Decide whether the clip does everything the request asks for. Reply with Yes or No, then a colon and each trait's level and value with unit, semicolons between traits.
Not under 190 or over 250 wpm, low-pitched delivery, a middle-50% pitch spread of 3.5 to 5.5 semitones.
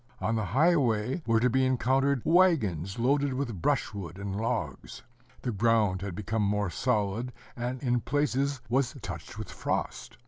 No: average, 150 wpm; low, 120 Hz; average, 4.4 semitones